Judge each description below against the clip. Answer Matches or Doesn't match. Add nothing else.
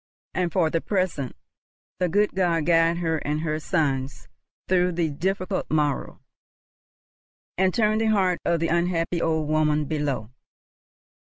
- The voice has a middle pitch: Matches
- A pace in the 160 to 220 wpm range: Doesn't match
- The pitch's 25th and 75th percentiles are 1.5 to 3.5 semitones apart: Matches